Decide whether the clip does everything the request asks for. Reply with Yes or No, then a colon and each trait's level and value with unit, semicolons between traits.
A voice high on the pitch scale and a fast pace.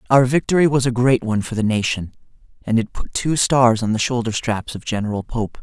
No: low, 120 Hz; fast, 225 wpm